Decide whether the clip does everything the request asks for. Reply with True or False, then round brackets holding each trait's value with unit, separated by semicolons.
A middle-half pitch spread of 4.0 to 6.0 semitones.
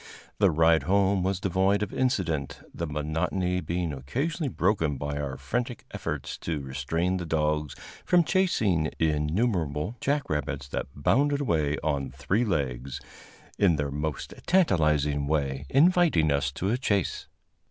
True (5.6 semitones)